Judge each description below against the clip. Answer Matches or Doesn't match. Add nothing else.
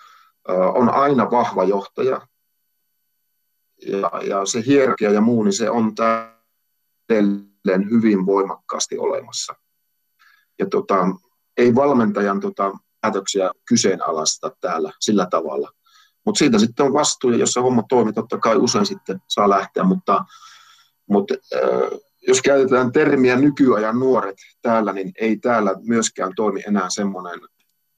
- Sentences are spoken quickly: Doesn't match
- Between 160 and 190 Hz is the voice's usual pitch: Doesn't match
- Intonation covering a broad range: Matches